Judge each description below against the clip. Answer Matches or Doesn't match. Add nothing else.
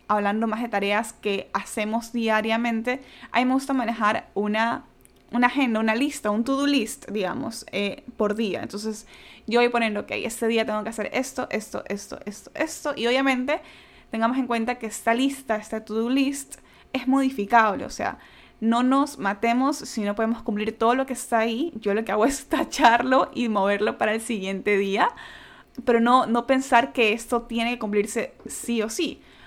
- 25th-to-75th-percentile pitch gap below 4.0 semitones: Matches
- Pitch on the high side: Matches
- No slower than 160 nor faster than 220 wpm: Matches